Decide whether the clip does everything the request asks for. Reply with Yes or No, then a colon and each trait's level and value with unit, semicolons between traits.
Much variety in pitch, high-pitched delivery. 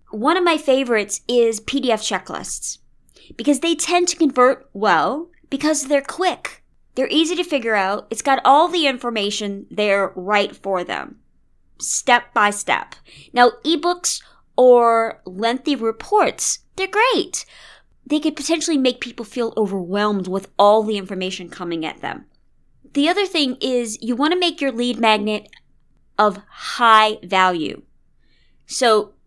Yes: wide, 6.6 semitones; high, 245 Hz